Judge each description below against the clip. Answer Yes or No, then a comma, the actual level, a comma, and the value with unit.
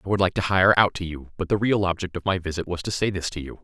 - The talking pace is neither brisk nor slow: No, fast, 345 wpm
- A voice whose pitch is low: Yes, very low, 90 Hz